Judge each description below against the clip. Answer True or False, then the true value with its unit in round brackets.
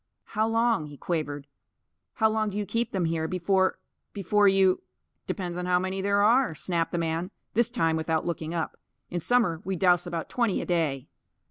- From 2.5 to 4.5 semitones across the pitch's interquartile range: True (3.9 semitones)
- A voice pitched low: False (180 Hz)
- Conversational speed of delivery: True (195 wpm)